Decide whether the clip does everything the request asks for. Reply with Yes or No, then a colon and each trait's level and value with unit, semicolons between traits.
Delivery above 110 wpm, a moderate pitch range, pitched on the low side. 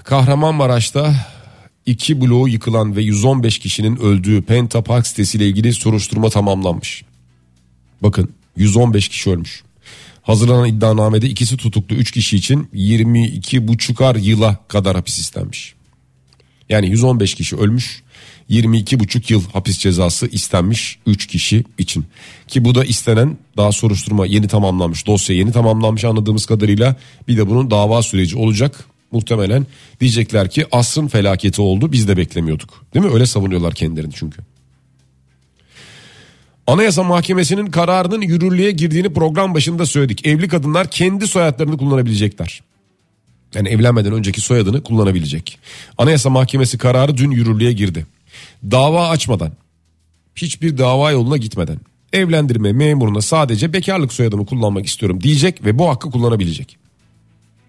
Yes: average, 125 wpm; average, 4.7 semitones; low, 115 Hz